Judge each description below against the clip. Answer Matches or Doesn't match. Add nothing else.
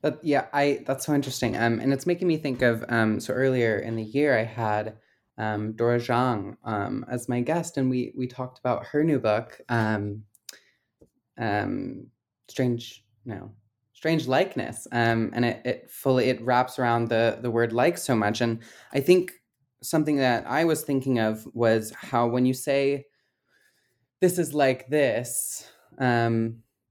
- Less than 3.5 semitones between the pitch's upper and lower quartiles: Matches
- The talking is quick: Doesn't match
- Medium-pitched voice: Doesn't match